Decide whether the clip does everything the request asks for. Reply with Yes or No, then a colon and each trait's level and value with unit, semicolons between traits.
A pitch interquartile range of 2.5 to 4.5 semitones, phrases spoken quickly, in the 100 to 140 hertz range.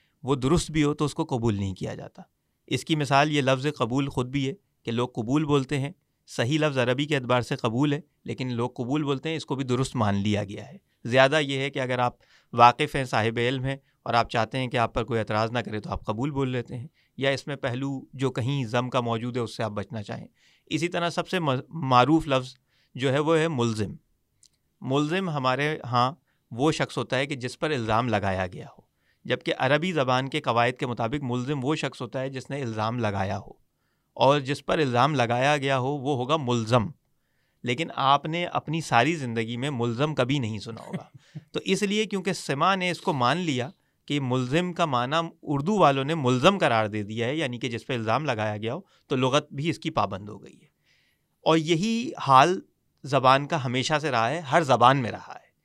Yes: average, 3.7 semitones; fast, 220 wpm; low, 135 Hz